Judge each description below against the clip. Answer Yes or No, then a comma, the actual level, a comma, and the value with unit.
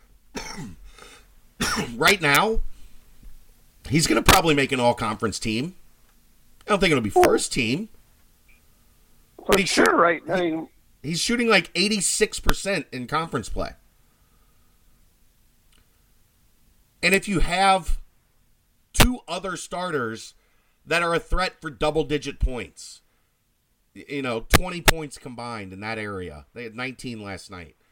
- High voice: No, medium, 140 Hz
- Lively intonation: Yes, wide, 7.4 semitones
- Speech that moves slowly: Yes, slow, 125 wpm